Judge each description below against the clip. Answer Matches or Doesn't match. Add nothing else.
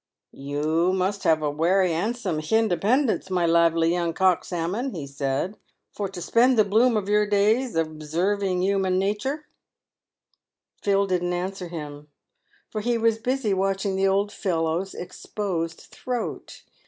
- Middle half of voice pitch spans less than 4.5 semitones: Matches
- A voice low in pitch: Doesn't match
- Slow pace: Doesn't match